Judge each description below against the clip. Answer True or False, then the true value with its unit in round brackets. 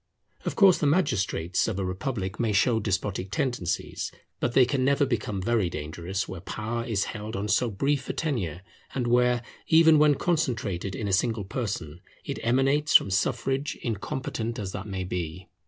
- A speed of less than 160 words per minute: False (170 wpm)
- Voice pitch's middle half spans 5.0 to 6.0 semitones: True (5.5 semitones)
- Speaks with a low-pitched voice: True (110 Hz)